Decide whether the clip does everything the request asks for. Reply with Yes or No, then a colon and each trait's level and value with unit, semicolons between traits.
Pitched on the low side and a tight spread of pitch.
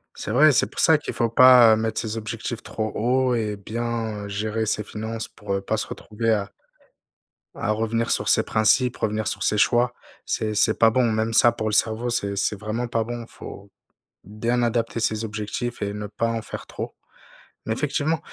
Yes: low, 110 Hz; narrow, 1.8 semitones